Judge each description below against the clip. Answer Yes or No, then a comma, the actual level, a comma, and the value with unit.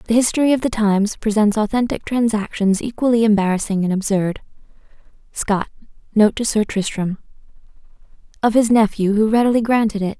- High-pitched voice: Yes, high, 215 Hz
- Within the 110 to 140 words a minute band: Yes, slow, 135 wpm